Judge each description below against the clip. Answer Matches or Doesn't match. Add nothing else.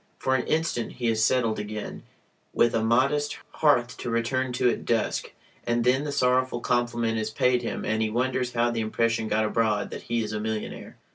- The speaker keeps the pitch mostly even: Matches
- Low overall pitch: Matches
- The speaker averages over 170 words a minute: Matches